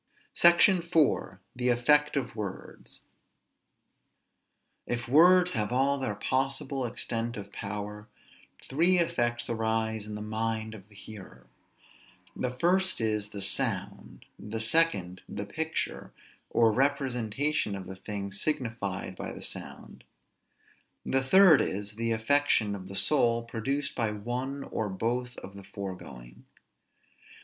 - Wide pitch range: No, average, 4.8 semitones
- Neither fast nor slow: No, slow, 130 wpm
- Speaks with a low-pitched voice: Yes, low, 115 Hz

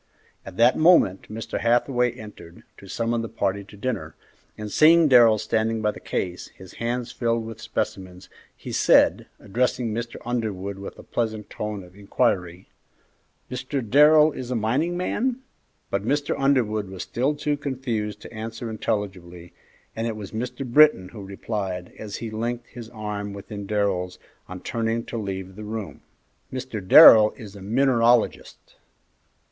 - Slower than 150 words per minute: No, average, 155 wpm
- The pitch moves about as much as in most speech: Yes, average, 3.4 semitones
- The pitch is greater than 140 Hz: No, low, 110 Hz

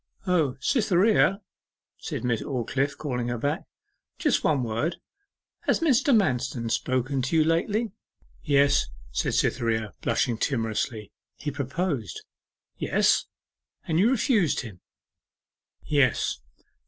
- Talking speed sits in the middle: No, slow, 110 wpm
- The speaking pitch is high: No, medium, 140 Hz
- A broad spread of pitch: Yes, wide, 6.5 semitones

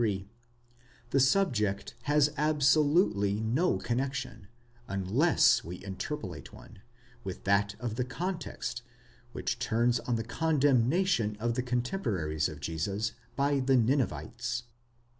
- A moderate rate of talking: No, slow, 115 wpm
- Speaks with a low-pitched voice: Yes, low, 120 Hz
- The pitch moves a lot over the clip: Yes, wide, 5.7 semitones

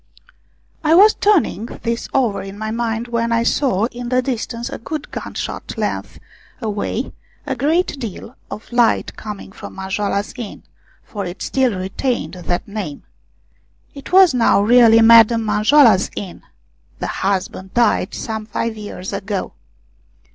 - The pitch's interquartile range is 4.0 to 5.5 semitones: No, average, 3.4 semitones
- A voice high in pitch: Yes, high, 225 Hz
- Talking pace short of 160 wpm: Yes, average, 145 wpm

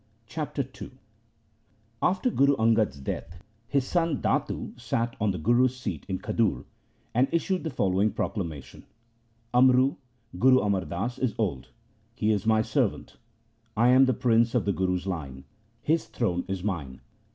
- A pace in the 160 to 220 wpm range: No, average, 150 wpm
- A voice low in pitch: Yes, low, 115 Hz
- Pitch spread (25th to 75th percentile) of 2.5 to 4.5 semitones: No, wide, 5.4 semitones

